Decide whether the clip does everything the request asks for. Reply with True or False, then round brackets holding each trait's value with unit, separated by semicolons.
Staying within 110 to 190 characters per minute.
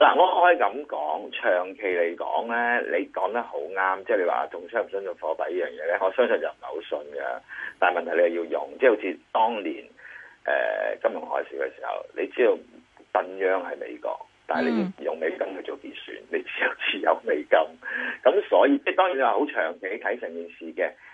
False (300 characters per minute)